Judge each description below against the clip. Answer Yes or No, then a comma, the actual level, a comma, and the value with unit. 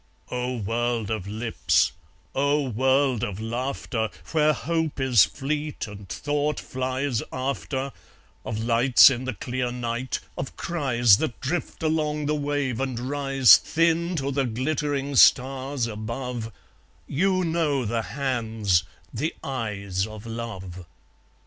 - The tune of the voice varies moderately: Yes, average, 3.8 semitones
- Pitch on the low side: Yes, low, 130 Hz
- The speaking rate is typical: No, slow, 125 wpm